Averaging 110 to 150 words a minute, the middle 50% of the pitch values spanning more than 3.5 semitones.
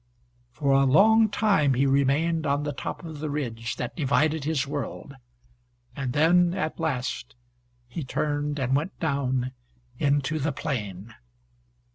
No: average, 140 wpm; average, 3.1 semitones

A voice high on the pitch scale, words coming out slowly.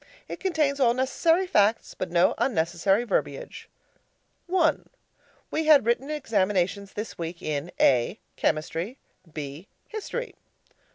Yes: high, 220 Hz; slow, 115 wpm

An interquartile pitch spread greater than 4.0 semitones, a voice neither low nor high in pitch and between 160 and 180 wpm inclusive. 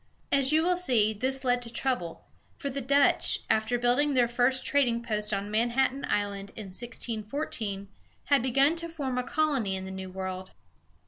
No: average, 4.7 semitones; high, 245 Hz; average, 175 wpm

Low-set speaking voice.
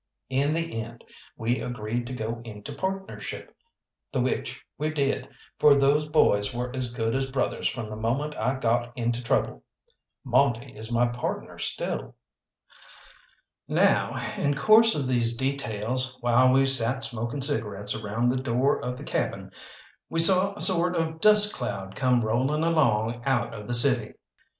Yes: low, 125 Hz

